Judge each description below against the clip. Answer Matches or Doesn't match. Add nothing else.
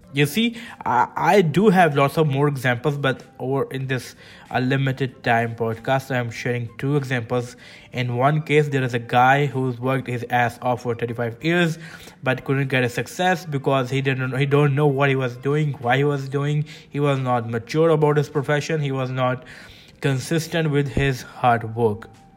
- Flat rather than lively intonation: Doesn't match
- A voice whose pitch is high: Doesn't match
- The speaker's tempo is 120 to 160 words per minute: Doesn't match